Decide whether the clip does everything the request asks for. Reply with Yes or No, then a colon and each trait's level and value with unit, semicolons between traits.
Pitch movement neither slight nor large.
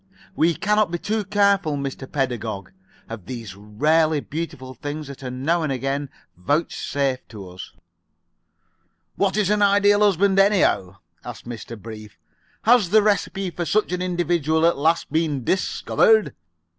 No: wide, 7.2 semitones